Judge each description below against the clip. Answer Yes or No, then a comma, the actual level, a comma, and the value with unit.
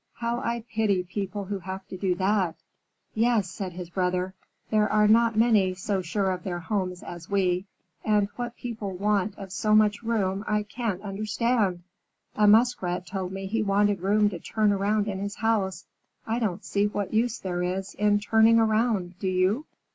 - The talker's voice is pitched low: No, high, 205 Hz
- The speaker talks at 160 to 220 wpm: Yes, average, 180 wpm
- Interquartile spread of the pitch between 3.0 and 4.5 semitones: No, narrow, 2.5 semitones